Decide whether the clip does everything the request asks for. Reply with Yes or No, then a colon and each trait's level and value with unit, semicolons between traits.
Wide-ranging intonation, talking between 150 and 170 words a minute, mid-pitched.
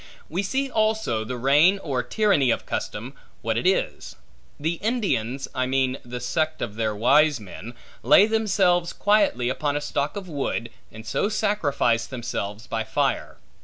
Yes: wide, 8.6 semitones; average, 160 wpm; medium, 145 Hz